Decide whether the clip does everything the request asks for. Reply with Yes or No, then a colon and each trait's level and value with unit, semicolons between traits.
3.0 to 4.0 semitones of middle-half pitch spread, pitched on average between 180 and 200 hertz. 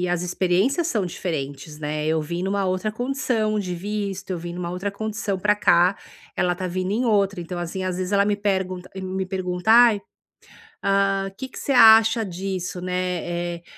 No: narrow, 2.6 semitones; high, 190 Hz